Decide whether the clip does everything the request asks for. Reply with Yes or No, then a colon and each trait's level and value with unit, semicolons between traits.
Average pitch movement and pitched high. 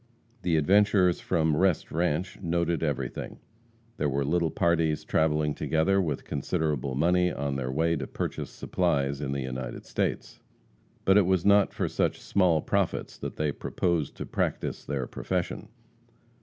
No: average, 3.8 semitones; very low, 80 Hz